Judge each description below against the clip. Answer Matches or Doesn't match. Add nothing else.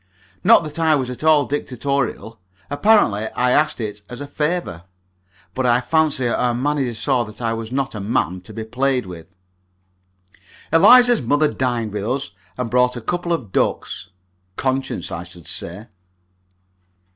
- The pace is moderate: Matches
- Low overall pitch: Matches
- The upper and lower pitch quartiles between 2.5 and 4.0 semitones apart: Doesn't match